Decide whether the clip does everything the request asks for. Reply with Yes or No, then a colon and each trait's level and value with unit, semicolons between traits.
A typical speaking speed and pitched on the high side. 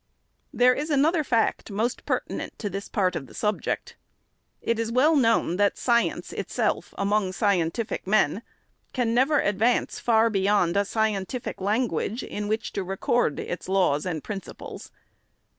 Yes: average, 145 wpm; high, 215 Hz